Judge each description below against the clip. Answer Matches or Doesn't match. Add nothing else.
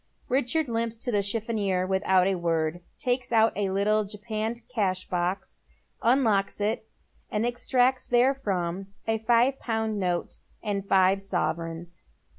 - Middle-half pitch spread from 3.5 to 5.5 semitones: Matches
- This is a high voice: Matches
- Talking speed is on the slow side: Matches